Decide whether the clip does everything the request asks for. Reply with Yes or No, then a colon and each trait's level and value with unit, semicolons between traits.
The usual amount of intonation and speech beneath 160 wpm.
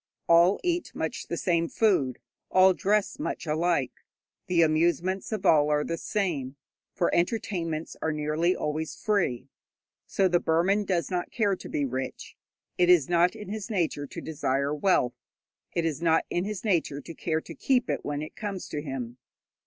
No: average, 4.0 semitones; average, 175 wpm